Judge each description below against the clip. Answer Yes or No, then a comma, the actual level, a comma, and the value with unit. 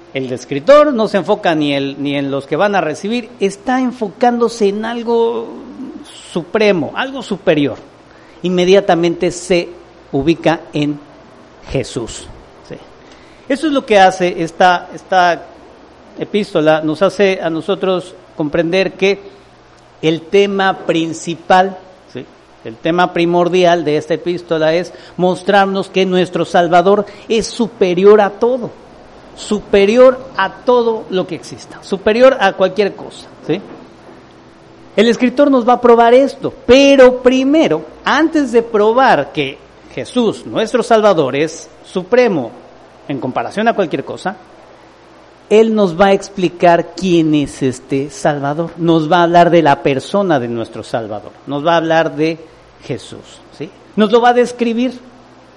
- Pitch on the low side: No, medium, 185 Hz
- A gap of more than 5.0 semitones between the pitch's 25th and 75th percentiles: Yes, wide, 5.4 semitones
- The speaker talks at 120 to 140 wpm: Yes, slow, 135 wpm